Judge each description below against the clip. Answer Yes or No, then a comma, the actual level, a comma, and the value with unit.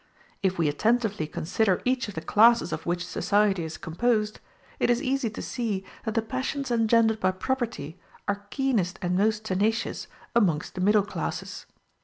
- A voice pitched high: Yes, high, 210 Hz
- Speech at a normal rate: Yes, average, 165 wpm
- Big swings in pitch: No, average, 4.0 semitones